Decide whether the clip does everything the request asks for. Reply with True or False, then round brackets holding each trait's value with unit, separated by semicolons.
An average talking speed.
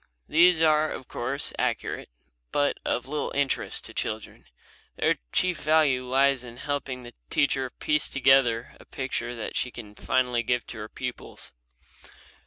True (155 wpm)